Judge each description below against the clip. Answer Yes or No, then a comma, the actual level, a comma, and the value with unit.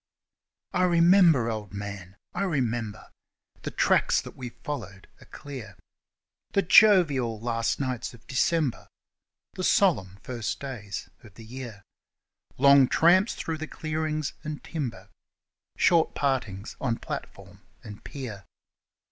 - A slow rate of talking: Yes, slow, 120 wpm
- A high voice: No, low, 130 Hz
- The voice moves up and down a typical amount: No, wide, 6.2 semitones